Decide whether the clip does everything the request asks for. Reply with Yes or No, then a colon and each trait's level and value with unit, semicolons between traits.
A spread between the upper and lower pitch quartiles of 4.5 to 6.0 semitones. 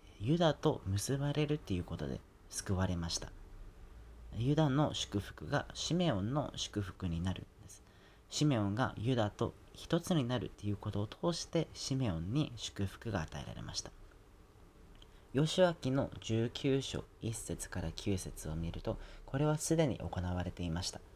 No: wide, 6.8 semitones